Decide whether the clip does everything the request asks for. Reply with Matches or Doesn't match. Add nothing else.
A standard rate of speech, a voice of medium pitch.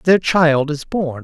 Matches